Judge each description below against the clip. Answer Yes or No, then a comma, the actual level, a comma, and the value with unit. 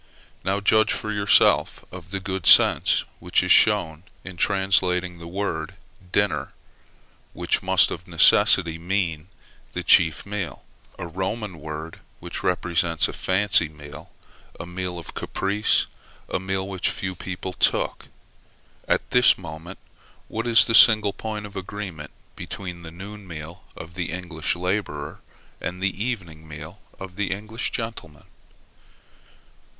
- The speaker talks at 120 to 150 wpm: Yes, average, 140 wpm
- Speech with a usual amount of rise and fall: Yes, average, 3.3 semitones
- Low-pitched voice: Yes, very low, 95 Hz